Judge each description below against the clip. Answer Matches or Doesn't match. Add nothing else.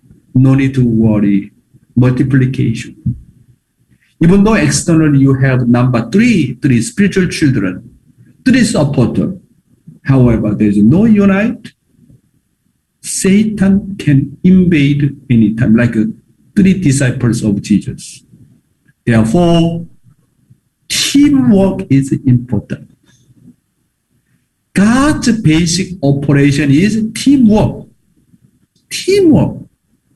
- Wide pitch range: Matches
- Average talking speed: Doesn't match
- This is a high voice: Doesn't match